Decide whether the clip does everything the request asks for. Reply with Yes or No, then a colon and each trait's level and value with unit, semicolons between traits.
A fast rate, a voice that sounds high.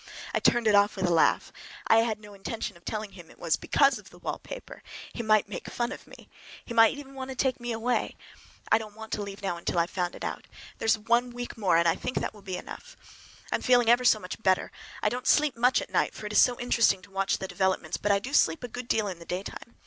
Yes: fast, 260 wpm; high, 215 Hz